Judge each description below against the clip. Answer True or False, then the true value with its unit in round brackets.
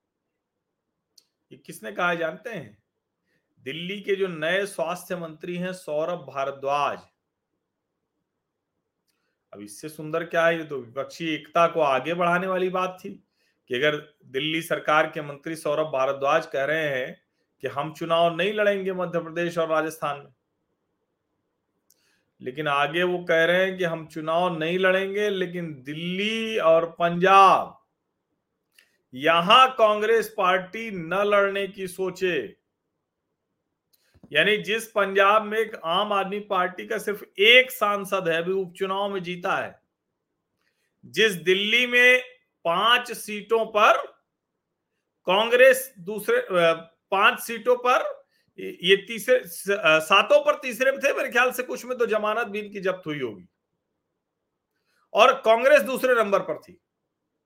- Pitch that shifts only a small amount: False (4.5 semitones)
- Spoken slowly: False (130 wpm)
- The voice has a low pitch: False (185 Hz)